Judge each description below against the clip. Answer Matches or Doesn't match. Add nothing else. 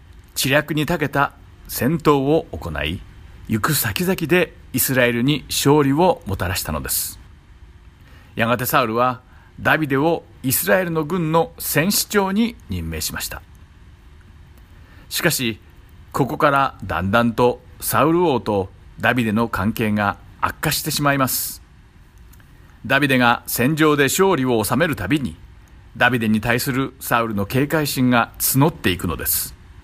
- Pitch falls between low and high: Doesn't match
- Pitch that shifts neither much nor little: Doesn't match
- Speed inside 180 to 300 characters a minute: Matches